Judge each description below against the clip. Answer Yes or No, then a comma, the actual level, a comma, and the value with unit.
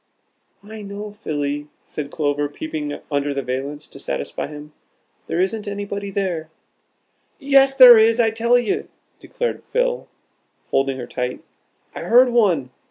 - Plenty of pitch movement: Yes, wide, 7.8 semitones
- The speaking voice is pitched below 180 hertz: No, high, 195 Hz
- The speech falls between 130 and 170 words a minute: Yes, average, 140 wpm